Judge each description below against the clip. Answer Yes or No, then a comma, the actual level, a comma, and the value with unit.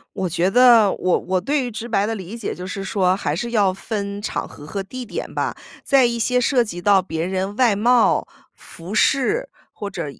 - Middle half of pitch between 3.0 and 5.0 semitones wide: Yes, average, 4.3 semitones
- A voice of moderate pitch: No, high, 205 Hz